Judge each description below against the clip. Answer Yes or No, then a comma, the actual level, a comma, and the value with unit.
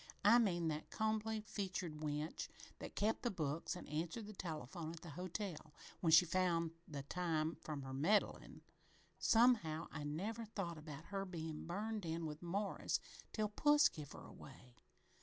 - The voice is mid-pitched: Yes, medium, 170 Hz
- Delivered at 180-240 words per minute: No, average, 160 wpm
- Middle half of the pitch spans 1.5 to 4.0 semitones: No, average, 5.0 semitones